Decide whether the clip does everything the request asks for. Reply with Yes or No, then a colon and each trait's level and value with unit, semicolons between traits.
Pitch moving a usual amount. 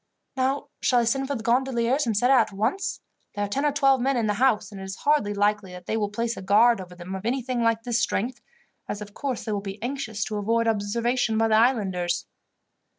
Yes: average, 3.9 semitones